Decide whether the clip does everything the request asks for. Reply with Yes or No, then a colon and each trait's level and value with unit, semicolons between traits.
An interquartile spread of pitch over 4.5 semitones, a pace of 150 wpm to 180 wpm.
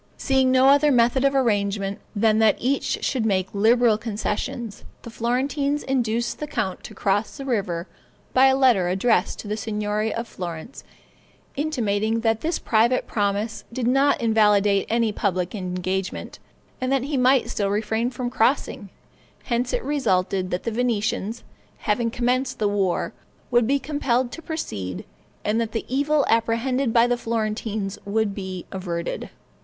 No: average, 4.0 semitones; average, 155 wpm